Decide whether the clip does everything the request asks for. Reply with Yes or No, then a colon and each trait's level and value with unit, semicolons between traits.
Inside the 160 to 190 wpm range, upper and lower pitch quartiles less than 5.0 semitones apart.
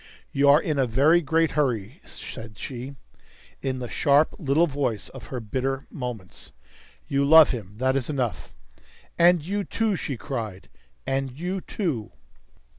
No: average, 150 wpm; average, 4.1 semitones